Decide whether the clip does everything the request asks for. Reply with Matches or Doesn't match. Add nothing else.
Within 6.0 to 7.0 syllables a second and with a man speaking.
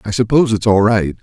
Matches